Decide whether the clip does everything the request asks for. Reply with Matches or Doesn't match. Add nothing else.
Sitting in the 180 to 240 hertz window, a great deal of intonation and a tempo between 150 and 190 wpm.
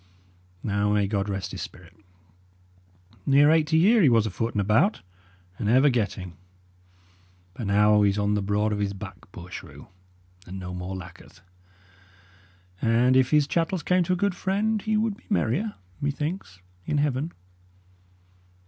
Doesn't match